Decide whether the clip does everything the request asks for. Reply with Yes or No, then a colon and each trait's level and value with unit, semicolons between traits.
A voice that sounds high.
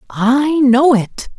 Yes: very high, 255 Hz